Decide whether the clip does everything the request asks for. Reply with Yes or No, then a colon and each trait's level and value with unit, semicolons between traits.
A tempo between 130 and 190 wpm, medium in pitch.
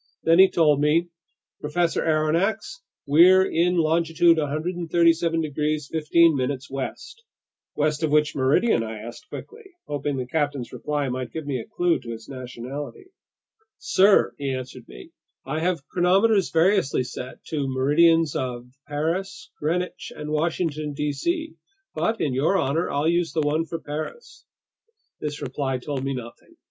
Yes: average, 145 wpm; medium, 155 Hz